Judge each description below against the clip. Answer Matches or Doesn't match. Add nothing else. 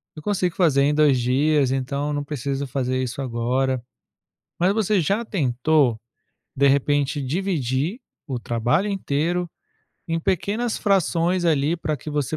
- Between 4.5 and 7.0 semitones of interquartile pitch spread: Matches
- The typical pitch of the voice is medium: Matches